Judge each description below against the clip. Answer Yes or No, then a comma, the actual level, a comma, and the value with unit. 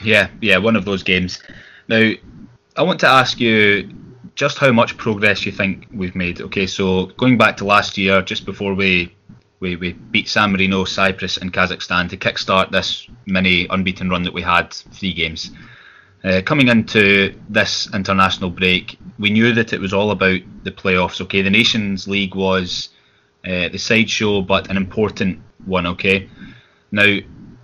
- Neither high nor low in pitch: No, very low, 95 Hz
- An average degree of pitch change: No, narrow, 2.2 semitones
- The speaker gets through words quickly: No, average, 170 wpm